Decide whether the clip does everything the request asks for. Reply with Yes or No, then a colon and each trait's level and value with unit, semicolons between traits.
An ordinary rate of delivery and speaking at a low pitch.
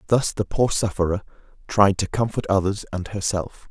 Yes: average, 160 wpm; low, 100 Hz